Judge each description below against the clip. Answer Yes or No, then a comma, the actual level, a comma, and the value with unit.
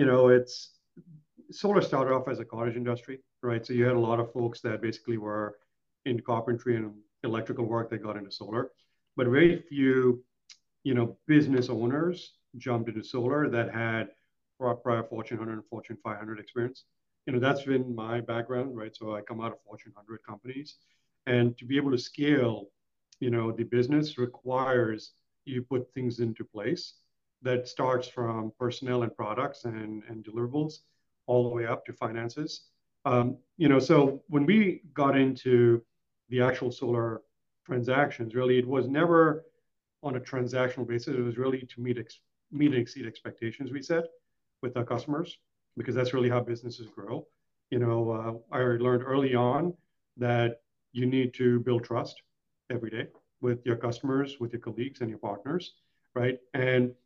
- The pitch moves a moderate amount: No, narrow, 2.3 semitones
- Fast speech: No, average, 170 wpm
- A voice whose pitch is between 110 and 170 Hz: Yes, low, 125 Hz